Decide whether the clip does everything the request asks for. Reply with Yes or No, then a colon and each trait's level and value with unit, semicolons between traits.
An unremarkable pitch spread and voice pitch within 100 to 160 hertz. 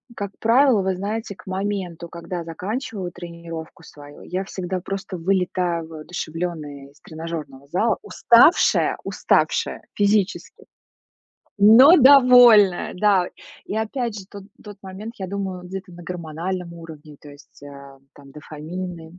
No: average, 3.6 semitones; medium, 180 Hz